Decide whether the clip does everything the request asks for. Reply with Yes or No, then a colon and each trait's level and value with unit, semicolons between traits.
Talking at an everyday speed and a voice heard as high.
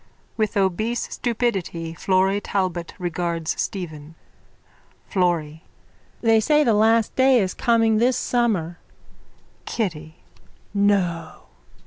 No: slow, 95 wpm; high, 195 Hz